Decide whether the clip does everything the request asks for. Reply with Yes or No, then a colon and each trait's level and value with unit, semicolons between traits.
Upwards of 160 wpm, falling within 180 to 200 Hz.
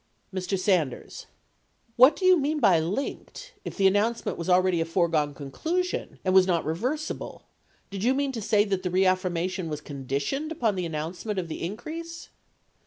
Yes: average, 180 wpm; high, 190 Hz